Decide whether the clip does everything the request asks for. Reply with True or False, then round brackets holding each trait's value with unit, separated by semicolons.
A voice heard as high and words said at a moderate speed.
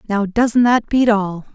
True (215 Hz; 195 wpm)